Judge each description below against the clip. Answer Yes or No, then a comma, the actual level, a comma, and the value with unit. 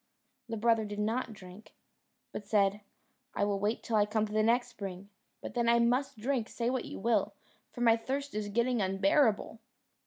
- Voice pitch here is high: Yes, high, 220 Hz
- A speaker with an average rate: Yes, average, 190 wpm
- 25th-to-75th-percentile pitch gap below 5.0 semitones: Yes, narrow, 2.5 semitones